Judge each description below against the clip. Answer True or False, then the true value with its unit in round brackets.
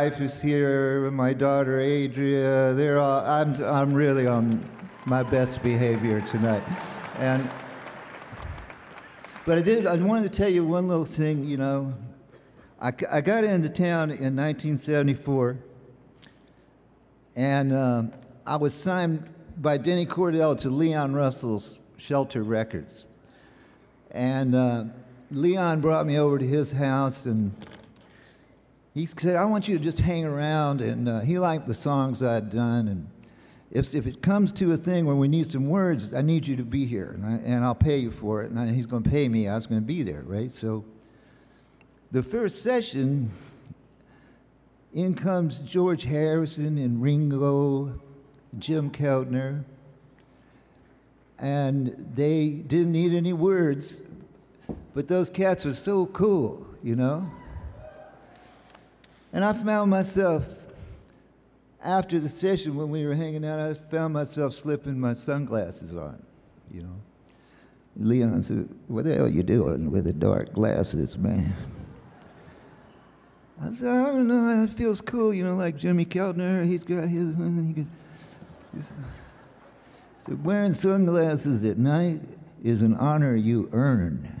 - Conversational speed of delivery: True (150 wpm)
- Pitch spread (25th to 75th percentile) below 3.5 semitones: False (4.6 semitones)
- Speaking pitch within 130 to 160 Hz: True (140 Hz)